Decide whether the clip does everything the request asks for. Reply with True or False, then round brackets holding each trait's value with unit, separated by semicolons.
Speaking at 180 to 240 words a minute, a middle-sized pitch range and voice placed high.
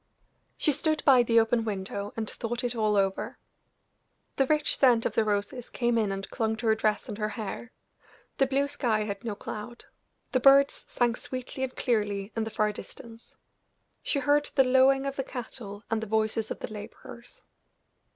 True (185 wpm; 3.5 semitones; 230 Hz)